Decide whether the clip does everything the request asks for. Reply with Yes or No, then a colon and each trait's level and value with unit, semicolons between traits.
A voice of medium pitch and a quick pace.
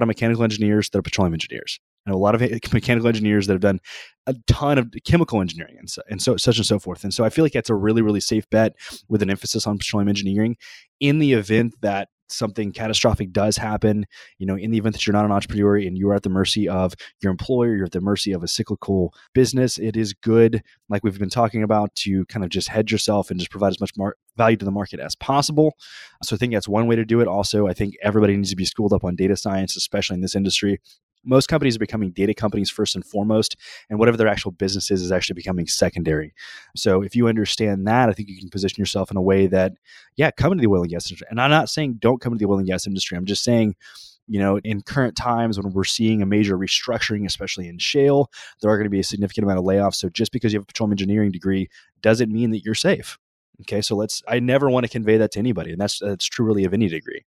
No: low, 105 Hz; fast, 260 wpm